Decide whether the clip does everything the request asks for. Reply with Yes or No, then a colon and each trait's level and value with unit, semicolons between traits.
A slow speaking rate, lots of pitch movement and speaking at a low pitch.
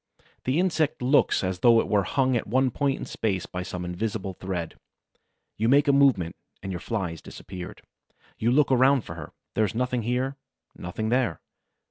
No: average, 185 wpm; wide, 6.0 semitones; low, 115 Hz